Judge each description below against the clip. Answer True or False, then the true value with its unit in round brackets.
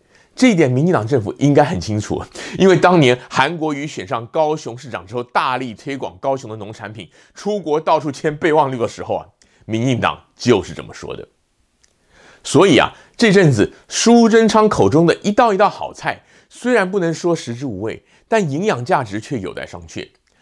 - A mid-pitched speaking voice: True (150 Hz)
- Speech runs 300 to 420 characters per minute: False (280 characters per minute)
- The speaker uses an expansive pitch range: True (6.8 semitones)